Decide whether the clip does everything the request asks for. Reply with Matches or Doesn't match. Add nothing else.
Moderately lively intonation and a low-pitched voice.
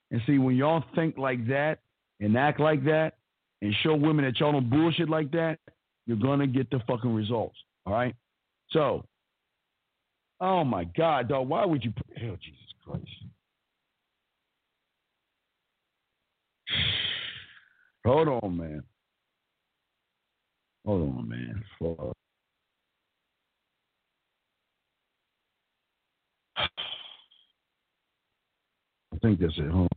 Doesn't match